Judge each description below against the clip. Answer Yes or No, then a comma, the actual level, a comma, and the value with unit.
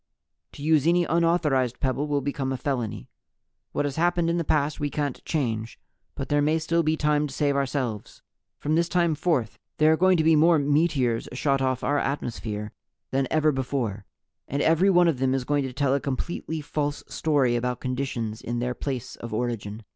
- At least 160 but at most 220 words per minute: Yes, average, 195 wpm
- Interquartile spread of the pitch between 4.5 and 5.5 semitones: No, average, 3.8 semitones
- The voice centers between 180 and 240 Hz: No, medium, 140 Hz